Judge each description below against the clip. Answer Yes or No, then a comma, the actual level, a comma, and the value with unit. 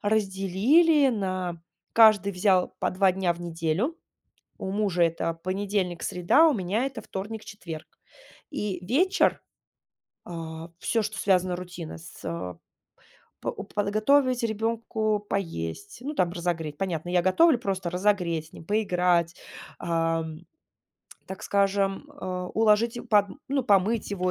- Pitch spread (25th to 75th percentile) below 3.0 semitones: No, average, 3.8 semitones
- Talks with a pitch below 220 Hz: Yes, high, 190 Hz